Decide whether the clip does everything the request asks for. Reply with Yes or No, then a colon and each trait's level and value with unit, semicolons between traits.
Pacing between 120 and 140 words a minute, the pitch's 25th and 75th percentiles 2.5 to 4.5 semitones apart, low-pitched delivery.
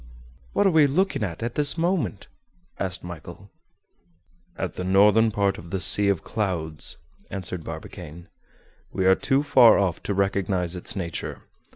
No: average, 155 wpm; average, 4.2 semitones; low, 100 Hz